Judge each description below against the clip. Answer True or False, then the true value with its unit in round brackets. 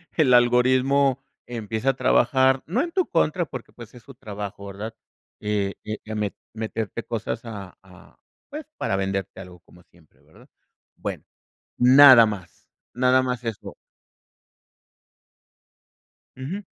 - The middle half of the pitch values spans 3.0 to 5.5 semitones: True (4.2 semitones)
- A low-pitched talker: True (115 Hz)